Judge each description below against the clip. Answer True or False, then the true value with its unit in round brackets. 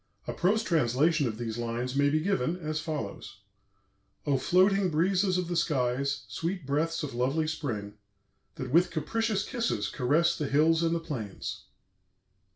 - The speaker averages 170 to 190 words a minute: False (155 wpm)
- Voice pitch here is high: False (155 Hz)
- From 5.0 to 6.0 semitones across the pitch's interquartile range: True (5.3 semitones)